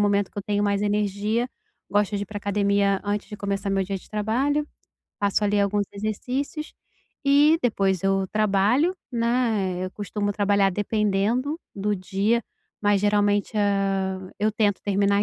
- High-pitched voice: Yes, high, 205 Hz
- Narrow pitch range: Yes, narrow, 1.4 semitones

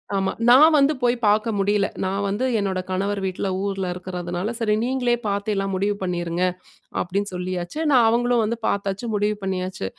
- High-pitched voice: Yes, high, 200 Hz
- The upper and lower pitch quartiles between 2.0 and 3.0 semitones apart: No, average, 3.4 semitones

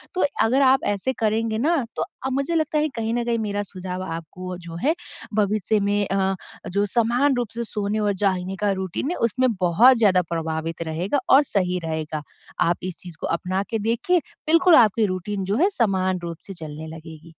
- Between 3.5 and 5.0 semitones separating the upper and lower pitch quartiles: Yes, average, 4.6 semitones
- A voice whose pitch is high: Yes, high, 200 Hz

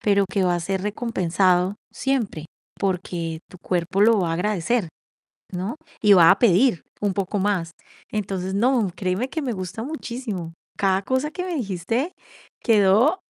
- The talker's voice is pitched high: Yes, high, 195 Hz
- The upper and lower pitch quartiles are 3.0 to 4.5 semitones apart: Yes, average, 4.2 semitones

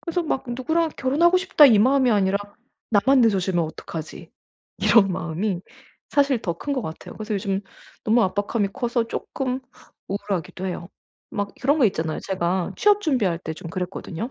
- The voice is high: Yes, high, 210 Hz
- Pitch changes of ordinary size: No, wide, 6.1 semitones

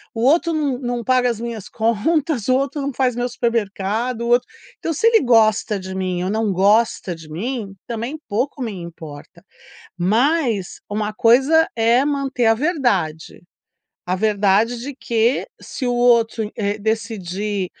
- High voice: Yes, high, 230 Hz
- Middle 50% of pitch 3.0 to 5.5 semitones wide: Yes, average, 3.9 semitones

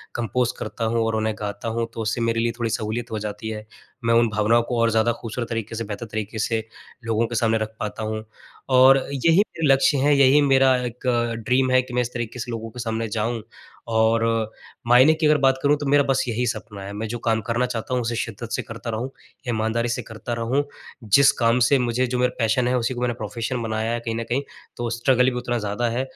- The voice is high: No, low, 115 Hz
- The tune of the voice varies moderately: No, narrow, 2.1 semitones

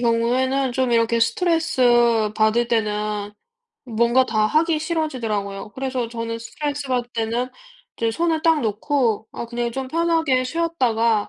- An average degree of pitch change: Yes, average, 3.4 semitones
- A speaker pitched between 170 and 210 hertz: No, high, 240 Hz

